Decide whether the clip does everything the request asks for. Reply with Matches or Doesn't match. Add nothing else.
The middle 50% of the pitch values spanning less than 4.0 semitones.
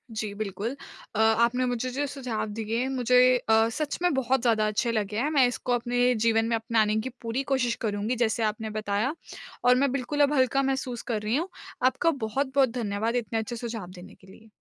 Matches